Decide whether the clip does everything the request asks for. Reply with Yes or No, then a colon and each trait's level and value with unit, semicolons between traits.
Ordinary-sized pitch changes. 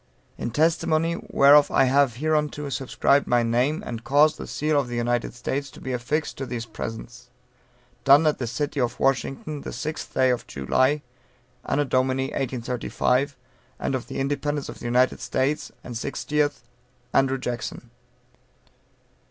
Yes: average, 3.1 semitones